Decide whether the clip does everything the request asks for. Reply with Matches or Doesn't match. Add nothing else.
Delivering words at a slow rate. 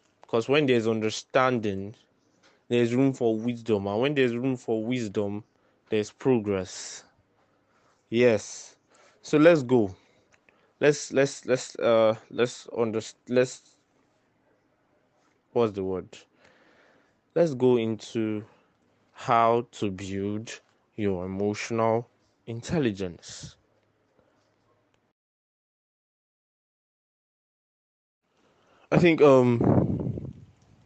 Matches